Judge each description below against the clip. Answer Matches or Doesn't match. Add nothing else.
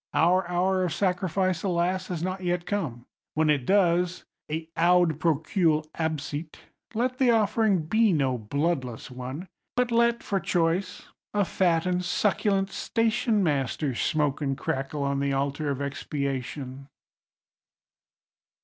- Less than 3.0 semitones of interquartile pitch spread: Doesn't match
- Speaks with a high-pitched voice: Doesn't match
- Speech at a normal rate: Doesn't match